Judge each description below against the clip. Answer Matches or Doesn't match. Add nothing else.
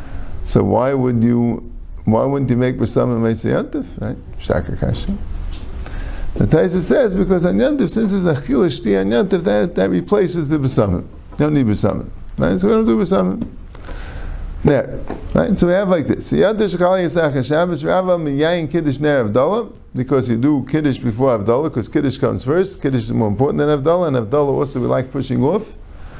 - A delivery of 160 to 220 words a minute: Doesn't match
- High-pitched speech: Doesn't match